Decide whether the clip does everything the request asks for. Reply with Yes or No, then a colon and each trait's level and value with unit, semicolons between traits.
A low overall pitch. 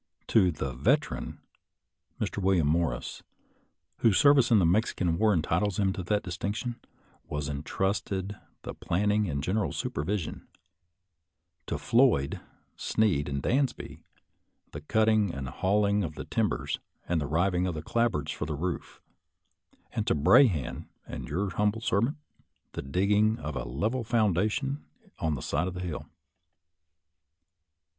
Yes: very low, 95 Hz